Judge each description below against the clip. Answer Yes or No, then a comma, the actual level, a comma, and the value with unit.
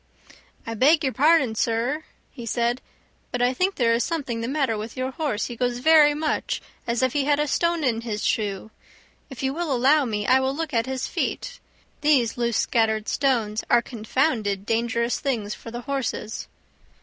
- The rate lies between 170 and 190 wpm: Yes, average, 185 wpm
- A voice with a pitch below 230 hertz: No, high, 245 Hz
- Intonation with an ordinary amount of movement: Yes, average, 3.9 semitones